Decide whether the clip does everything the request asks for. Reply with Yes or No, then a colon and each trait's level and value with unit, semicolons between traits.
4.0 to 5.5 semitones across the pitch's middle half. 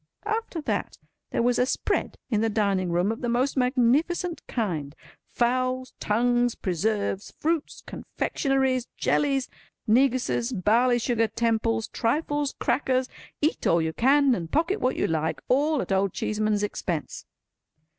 Yes: average, 4.3 semitones